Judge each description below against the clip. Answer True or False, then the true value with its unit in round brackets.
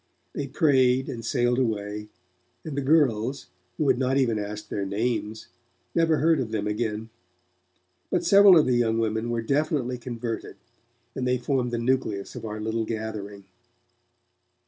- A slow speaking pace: False (155 wpm)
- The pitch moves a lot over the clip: False (3.3 semitones)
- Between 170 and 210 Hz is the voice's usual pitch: False (120 Hz)